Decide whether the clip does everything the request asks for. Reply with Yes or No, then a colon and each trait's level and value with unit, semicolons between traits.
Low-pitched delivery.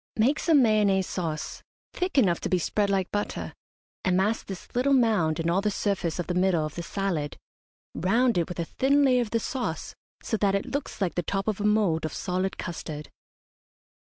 No: high, 195 Hz